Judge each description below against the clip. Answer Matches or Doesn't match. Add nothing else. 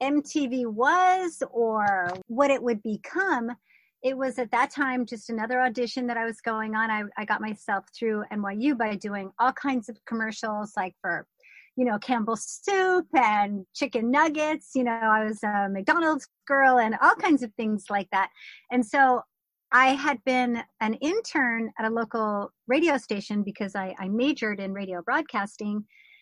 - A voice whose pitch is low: Doesn't match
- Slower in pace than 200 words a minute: Matches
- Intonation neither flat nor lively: Matches